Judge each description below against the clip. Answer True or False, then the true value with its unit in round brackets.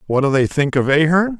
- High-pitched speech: False (155 Hz)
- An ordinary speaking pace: False (260 wpm)